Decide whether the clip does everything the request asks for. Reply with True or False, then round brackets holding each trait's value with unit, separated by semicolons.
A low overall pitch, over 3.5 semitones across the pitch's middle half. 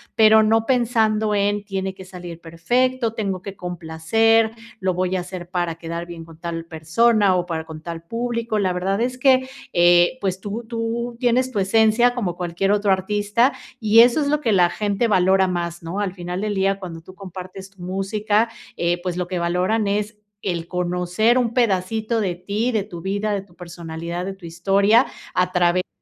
False (195 Hz; 3.9 semitones)